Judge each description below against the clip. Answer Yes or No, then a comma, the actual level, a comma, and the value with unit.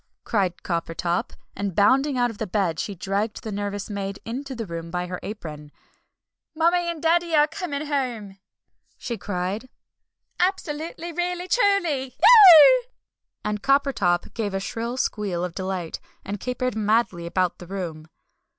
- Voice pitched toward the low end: No, high, 220 Hz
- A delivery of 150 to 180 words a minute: No, average, 140 wpm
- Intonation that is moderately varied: No, wide, 7.8 semitones